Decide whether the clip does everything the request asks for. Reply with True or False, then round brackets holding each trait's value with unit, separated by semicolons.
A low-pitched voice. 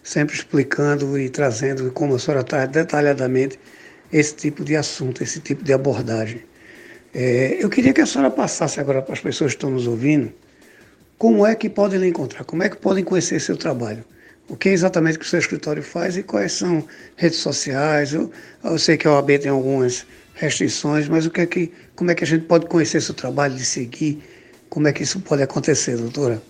False (150 Hz)